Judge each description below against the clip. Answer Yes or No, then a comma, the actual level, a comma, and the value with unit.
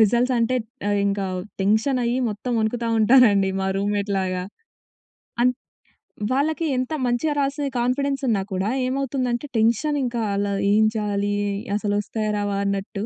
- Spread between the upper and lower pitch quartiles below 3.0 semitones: No, average, 3.8 semitones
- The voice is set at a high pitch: Yes, high, 220 Hz